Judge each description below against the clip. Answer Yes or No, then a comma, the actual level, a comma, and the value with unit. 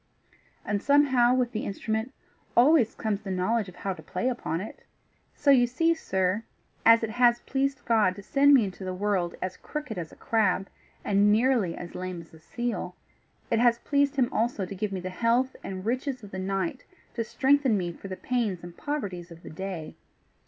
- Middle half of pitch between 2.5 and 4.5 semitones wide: No, average, 5.1 semitones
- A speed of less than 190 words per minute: No, average, 200 wpm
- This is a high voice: Yes, high, 220 Hz